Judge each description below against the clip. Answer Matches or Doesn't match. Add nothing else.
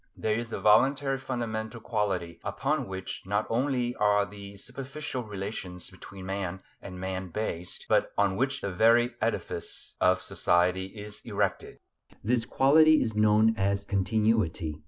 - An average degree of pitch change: Matches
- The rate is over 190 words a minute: Doesn't match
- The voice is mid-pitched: Doesn't match